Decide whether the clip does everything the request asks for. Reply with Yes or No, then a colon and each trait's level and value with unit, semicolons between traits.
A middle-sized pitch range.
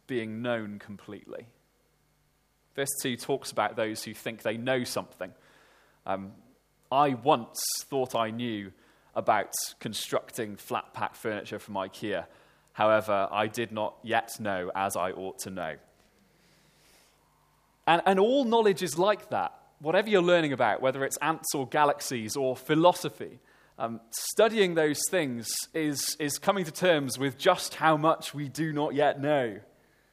No: wide, 5.8 semitones